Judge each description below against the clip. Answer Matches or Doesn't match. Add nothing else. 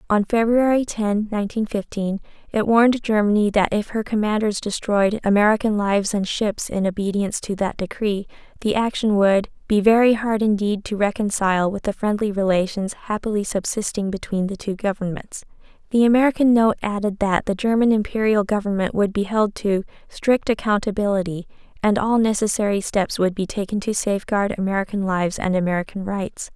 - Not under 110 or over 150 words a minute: Doesn't match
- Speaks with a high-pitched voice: Matches